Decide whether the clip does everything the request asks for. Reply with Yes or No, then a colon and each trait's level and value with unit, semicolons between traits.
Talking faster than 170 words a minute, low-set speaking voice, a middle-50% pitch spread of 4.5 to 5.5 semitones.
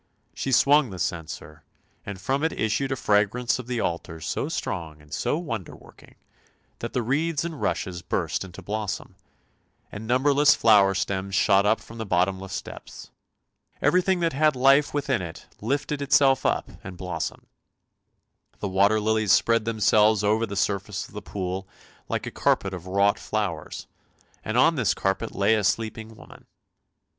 No: average, 160 wpm; low, 110 Hz; average, 5.1 semitones